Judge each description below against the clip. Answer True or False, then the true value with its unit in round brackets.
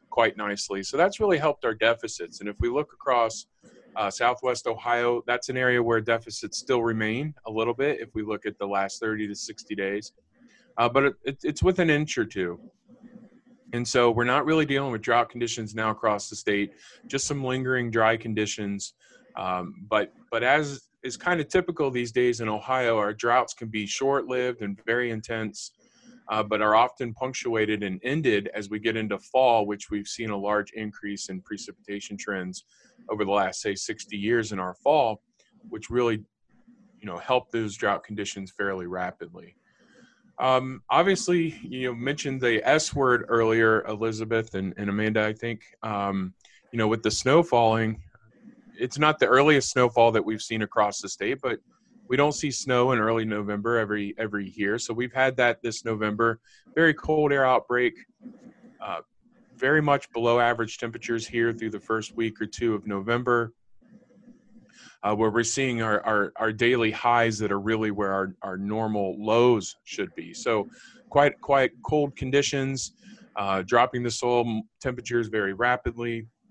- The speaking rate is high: False (175 wpm)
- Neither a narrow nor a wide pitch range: True (3.8 semitones)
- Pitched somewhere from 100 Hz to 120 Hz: True (115 Hz)